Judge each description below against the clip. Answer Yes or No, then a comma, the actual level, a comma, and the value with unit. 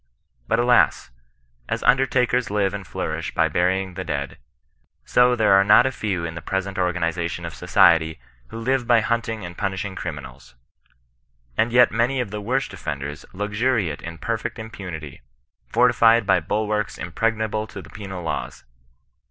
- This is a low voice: Yes, low, 105 Hz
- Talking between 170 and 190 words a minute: No, average, 160 wpm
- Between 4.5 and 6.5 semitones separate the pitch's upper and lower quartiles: Yes, average, 4.8 semitones